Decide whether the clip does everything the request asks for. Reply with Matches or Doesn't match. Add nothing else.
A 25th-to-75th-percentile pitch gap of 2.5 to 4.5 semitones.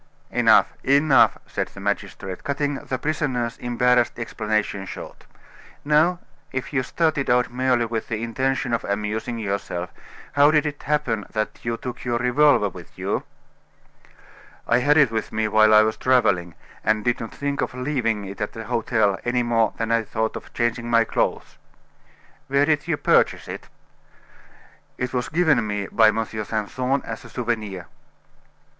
Matches